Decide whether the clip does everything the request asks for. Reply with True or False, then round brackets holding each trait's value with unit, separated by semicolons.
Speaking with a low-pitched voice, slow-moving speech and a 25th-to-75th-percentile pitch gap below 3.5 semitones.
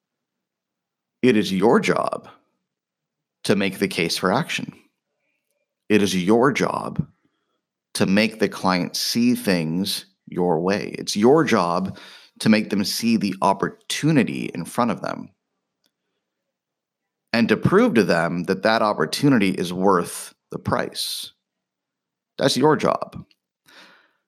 True (100 Hz; 125 wpm; 2.9 semitones)